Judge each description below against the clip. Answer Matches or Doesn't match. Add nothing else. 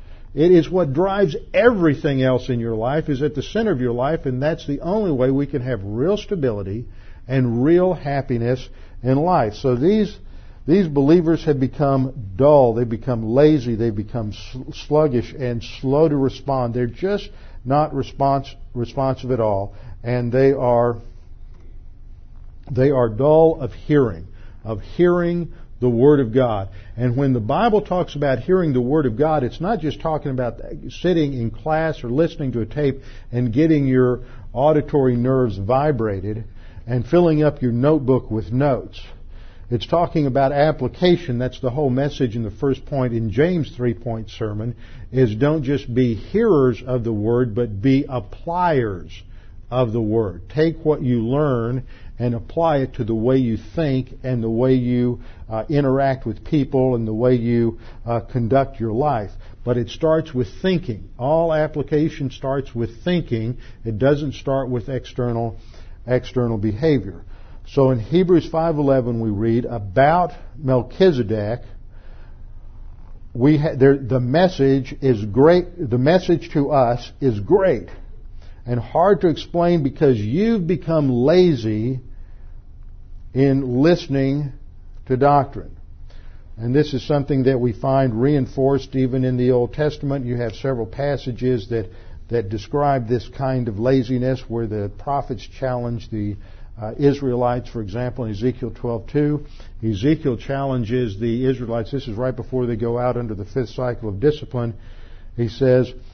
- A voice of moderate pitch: Doesn't match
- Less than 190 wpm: Matches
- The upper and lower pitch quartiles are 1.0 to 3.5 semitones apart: Doesn't match